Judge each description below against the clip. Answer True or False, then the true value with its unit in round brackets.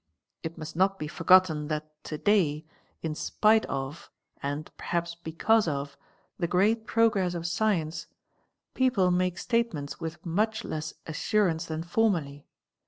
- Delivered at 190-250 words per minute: False (135 wpm)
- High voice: False (170 Hz)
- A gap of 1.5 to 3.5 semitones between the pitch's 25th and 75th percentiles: False (4.7 semitones)